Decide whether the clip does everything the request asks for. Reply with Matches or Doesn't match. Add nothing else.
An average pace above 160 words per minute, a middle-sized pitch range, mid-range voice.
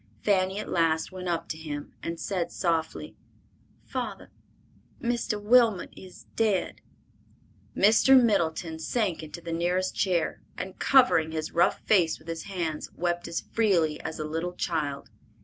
Doesn't match